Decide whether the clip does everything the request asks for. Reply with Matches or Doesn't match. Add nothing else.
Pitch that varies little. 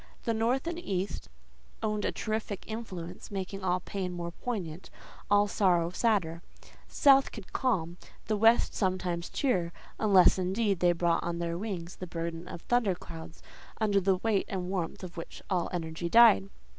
Doesn't match